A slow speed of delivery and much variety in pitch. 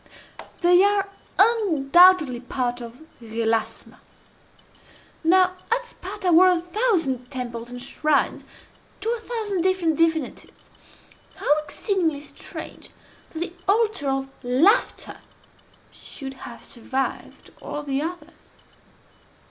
Yes: slow, 105 wpm; wide, 6.0 semitones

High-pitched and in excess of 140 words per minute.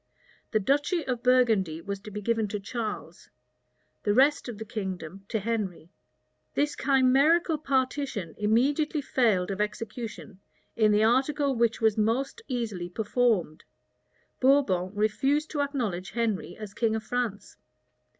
No: high, 225 Hz; slow, 135 wpm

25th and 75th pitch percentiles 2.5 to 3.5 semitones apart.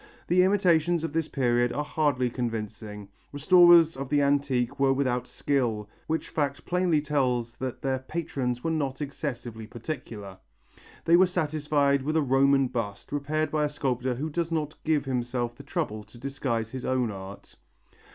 No: average, 4.1 semitones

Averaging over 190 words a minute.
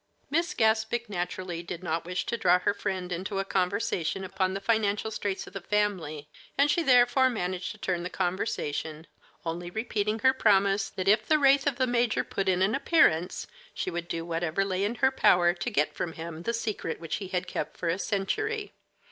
Yes: average, 200 wpm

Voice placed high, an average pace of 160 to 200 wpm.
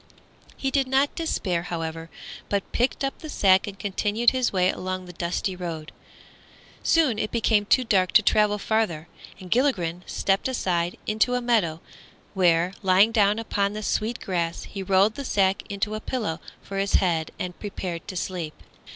Yes: high, 195 Hz; average, 170 wpm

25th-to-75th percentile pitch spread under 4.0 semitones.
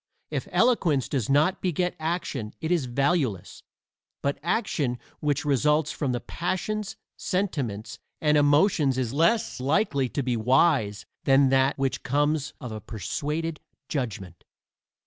No: average, 4.3 semitones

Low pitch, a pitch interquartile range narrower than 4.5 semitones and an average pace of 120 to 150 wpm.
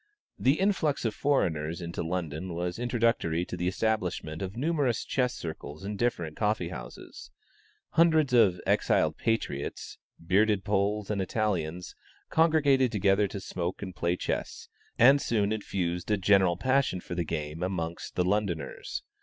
No: very low, 95 Hz; average, 5.1 semitones; average, 145 wpm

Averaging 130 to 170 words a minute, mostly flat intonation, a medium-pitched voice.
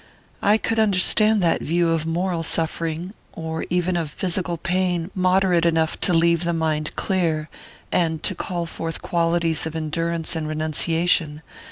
Yes: average, 150 wpm; narrow, 1.8 semitones; medium, 170 Hz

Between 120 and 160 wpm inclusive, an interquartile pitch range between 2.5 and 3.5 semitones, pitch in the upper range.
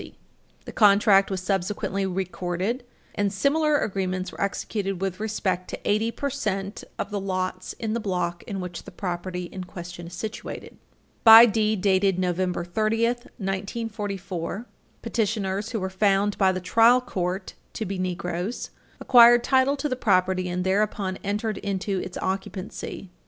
Yes: average, 145 wpm; average, 2.8 semitones; high, 195 Hz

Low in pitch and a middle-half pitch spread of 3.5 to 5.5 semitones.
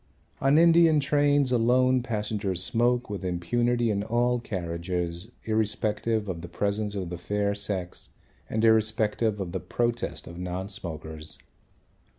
Yes: low, 105 Hz; average, 4.7 semitones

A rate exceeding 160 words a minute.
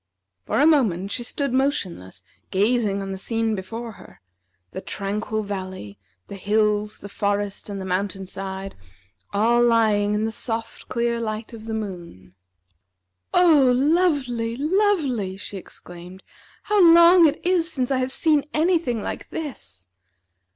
No: average, 145 wpm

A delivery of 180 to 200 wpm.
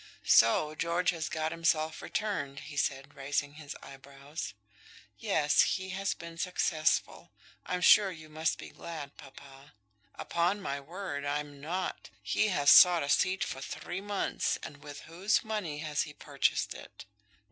No: average, 150 wpm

